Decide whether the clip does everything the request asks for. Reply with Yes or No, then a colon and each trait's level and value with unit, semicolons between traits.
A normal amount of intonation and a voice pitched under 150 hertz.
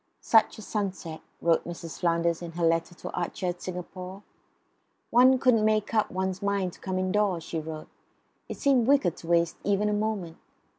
No: average, 3.7 semitones; medium, 185 Hz